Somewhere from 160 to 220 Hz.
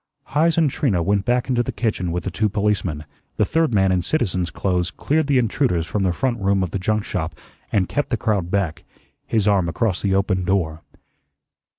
No: low, 100 Hz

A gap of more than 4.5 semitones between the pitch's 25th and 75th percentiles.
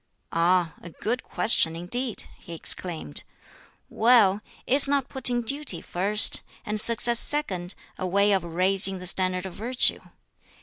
Yes: average, 5.1 semitones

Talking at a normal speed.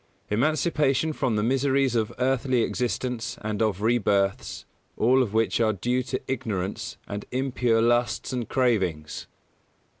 No: slow, 130 wpm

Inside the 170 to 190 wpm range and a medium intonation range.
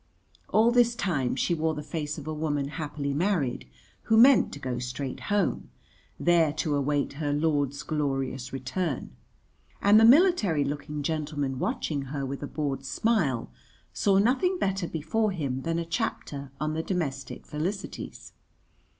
No: average, 150 wpm; average, 4.9 semitones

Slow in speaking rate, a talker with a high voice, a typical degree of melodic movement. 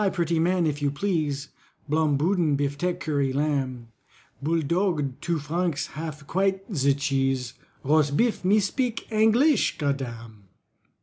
No: slow, 120 wpm; medium, 150 Hz; average, 4.4 semitones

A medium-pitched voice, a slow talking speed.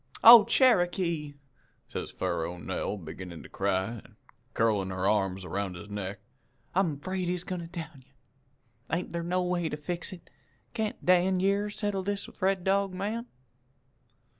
No: medium, 175 Hz; average, 160 wpm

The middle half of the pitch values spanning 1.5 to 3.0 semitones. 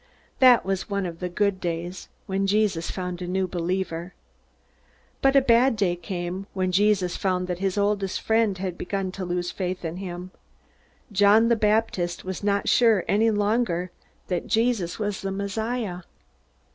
Yes: average, 2.7 semitones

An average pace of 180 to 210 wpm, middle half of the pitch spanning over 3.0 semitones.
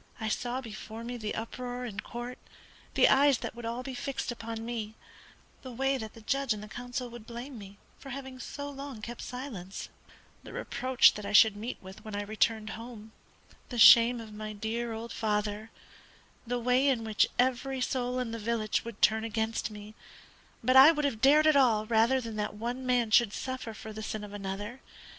No: average, 200 wpm; average, 2.7 semitones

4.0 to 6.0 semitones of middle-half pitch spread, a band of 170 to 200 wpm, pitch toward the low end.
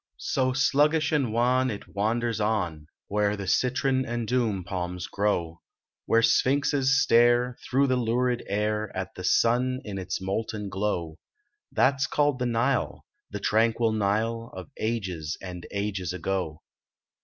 No: average, 4.5 semitones; average, 145 wpm; low, 110 Hz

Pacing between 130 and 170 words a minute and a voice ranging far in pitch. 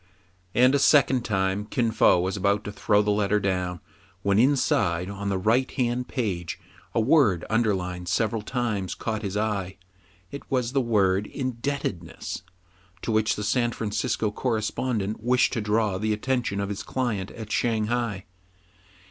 No: average, 160 wpm; average, 3.4 semitones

